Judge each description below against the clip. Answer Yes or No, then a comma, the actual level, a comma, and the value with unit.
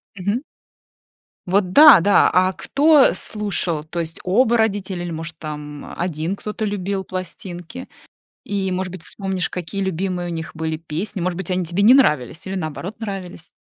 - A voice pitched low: No, medium, 185 Hz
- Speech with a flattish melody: No, average, 3.2 semitones